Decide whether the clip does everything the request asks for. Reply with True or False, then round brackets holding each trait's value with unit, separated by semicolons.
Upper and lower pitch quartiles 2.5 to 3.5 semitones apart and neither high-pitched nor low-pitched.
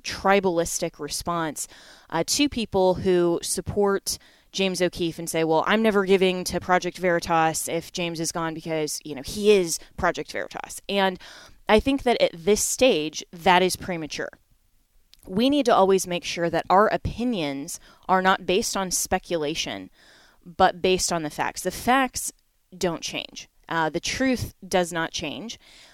True (3.0 semitones; 180 Hz)